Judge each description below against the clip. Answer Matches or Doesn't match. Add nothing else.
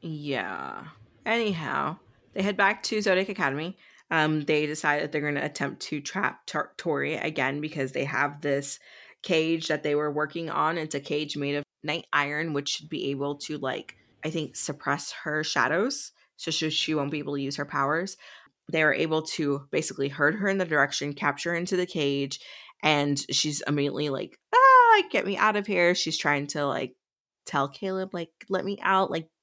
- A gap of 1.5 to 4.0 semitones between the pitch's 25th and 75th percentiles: Matches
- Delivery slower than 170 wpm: Doesn't match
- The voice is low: Doesn't match